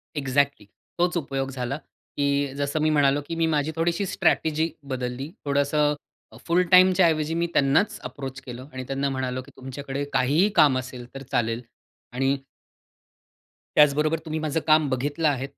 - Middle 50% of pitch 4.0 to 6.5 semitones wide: No, average, 2.8 semitones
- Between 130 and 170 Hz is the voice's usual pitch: Yes, medium, 140 Hz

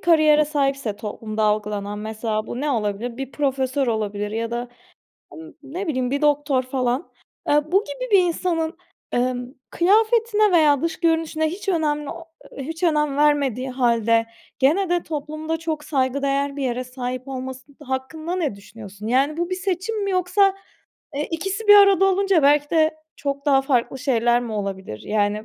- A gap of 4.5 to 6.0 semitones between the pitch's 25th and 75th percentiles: Yes, average, 5.1 semitones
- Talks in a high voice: Yes, very high, 280 Hz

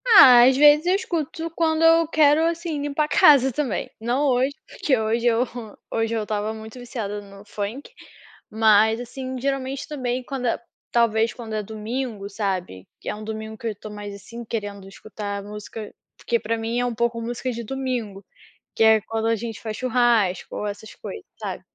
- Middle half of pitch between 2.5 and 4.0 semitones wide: Yes, average, 3.7 semitones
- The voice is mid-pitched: No, high, 230 Hz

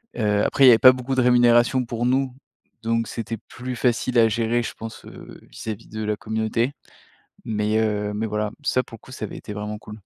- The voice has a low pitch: Yes, low, 115 Hz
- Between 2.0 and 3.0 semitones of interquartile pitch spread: Yes, narrow, 2.4 semitones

